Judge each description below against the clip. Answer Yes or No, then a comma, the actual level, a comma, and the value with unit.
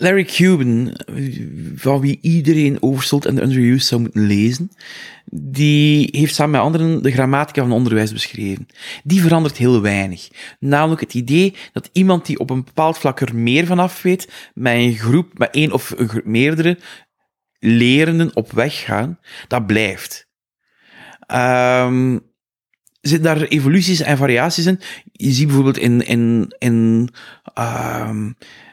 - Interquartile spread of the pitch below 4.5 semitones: No, average, 5.2 semitones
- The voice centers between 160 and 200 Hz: No, low, 135 Hz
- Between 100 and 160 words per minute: Yes, average, 145 wpm